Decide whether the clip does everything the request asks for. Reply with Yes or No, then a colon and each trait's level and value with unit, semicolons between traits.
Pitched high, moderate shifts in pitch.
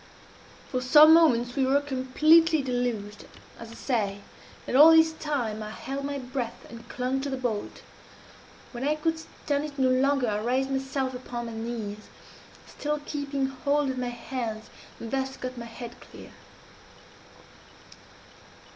Yes: very high, 260 Hz; average, 3.1 semitones